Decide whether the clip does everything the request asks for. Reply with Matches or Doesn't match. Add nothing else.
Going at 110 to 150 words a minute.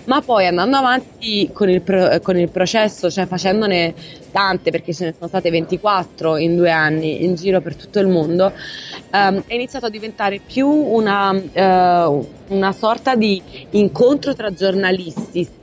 Doesn't match